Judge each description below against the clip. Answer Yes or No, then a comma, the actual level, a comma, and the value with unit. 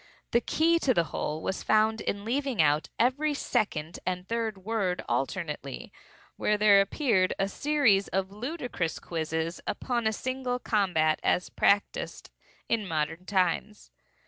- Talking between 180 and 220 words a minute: No, average, 140 wpm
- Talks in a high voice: Yes, high, 200 Hz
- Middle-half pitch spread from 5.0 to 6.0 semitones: Yes, wide, 5.6 semitones